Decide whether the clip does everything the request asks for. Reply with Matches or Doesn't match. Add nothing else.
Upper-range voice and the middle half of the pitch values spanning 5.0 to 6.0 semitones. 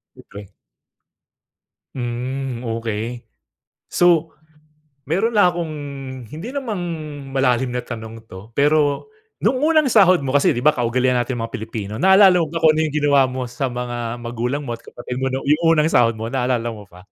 Doesn't match